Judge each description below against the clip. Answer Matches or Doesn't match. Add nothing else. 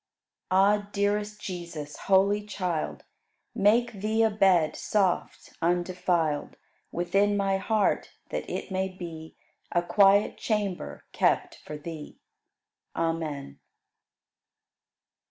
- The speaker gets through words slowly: Matches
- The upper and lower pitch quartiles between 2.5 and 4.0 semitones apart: Matches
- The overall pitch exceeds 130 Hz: Matches